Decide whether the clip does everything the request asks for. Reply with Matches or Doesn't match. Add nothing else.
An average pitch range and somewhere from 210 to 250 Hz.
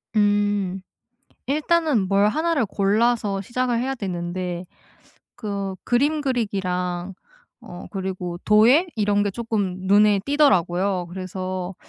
Doesn't match